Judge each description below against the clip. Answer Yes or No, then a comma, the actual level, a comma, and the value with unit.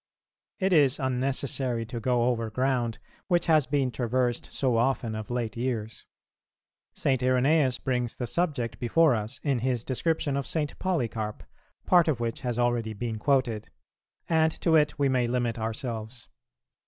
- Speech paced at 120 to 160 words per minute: Yes, average, 155 wpm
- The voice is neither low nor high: No, low, 125 Hz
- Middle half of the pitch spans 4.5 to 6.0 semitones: No, average, 3.1 semitones